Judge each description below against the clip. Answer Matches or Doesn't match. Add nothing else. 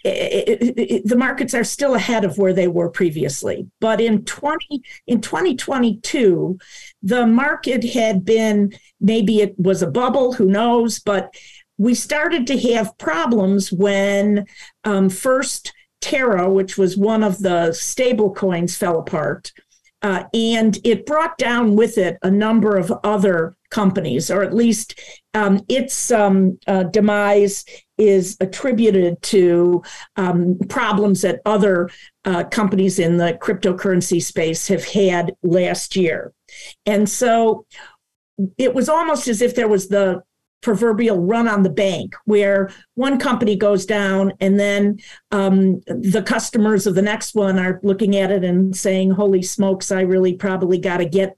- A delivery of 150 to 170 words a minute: Matches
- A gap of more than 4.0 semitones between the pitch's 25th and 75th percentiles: Doesn't match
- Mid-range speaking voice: Doesn't match